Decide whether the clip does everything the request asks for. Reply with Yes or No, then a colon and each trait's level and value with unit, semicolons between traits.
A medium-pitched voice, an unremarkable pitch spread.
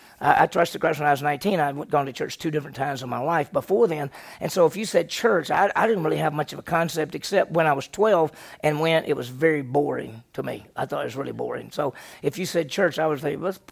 Yes: medium, 155 Hz; average, 3.0 semitones